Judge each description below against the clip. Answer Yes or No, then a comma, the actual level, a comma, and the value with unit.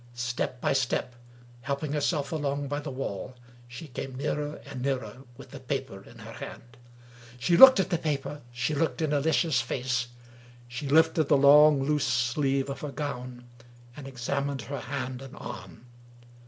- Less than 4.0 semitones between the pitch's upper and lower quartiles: Yes, average, 2.8 semitones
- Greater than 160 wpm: Yes, average, 170 wpm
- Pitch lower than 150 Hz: Yes, medium, 140 Hz